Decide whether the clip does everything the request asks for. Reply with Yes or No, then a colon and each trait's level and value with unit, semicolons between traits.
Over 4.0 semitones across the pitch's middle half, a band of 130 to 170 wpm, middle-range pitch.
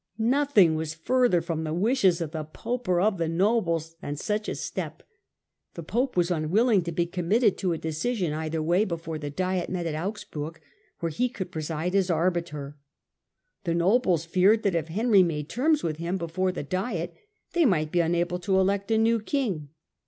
No: average, 4.4 semitones; average, 190 wpm; medium, 175 Hz